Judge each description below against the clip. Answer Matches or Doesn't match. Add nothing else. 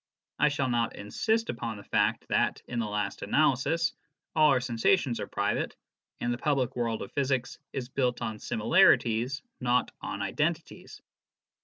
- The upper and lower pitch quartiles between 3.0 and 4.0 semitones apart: Matches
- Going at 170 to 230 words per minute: Doesn't match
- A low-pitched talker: Matches